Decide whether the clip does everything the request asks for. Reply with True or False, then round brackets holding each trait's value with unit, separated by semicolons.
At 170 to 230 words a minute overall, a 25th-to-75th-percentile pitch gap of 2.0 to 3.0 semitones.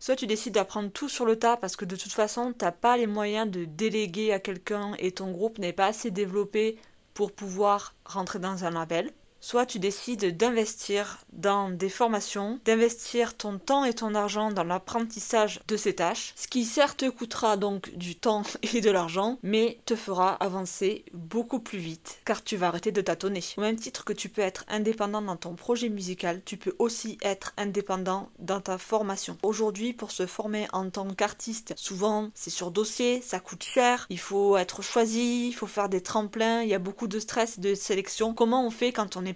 True (205 wpm; 2.7 semitones)